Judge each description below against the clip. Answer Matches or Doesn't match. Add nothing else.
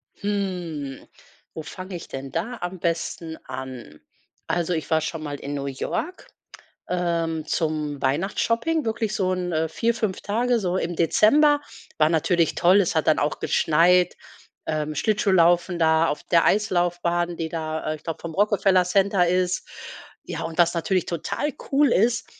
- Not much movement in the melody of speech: Doesn't match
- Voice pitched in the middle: Matches